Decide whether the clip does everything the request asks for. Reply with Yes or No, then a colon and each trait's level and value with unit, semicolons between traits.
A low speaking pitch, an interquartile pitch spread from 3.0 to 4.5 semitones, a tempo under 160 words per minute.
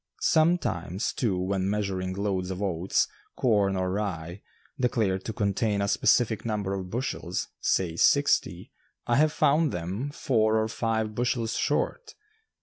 Yes: low, 105 Hz; average, 3.7 semitones; average, 140 wpm